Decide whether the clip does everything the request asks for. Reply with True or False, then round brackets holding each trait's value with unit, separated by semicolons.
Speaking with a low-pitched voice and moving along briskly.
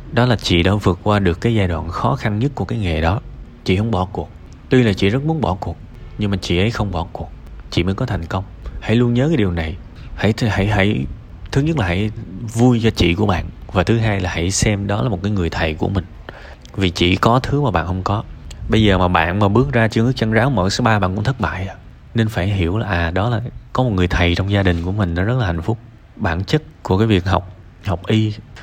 True (100 Hz; 265 wpm)